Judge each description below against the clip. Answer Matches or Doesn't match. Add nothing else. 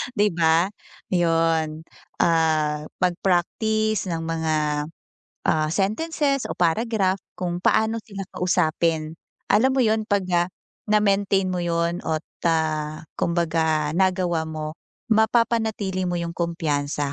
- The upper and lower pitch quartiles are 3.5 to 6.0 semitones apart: Matches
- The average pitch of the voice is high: Doesn't match